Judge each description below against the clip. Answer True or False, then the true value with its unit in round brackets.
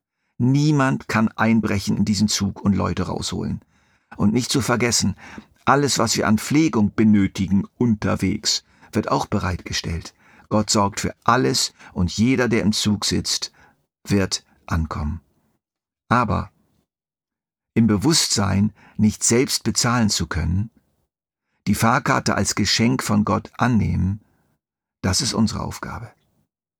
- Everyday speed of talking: False (120 wpm)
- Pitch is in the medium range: False (105 Hz)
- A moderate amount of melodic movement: True (3.4 semitones)